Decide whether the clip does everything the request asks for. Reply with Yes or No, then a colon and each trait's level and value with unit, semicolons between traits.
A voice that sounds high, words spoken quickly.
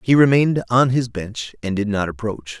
No: low, 115 Hz; fast, 210 wpm